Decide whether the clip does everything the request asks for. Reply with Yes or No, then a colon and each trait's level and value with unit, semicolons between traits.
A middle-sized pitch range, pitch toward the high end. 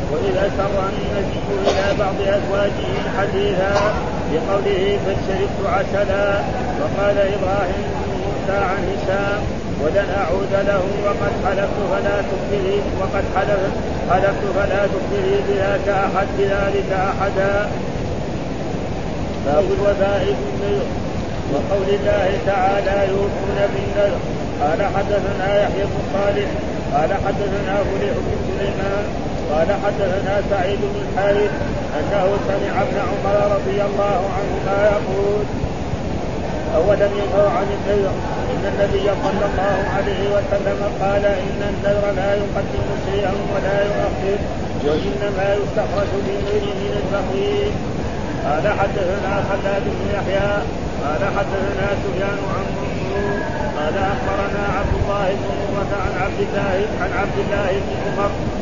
No: narrow, 0.8 semitones; high, 195 Hz